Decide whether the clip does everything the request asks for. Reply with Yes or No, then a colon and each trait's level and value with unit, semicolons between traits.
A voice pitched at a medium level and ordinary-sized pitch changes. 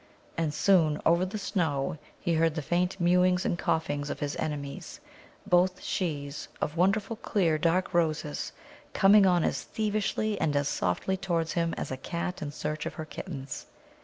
Yes: medium, 170 Hz; average, 3.7 semitones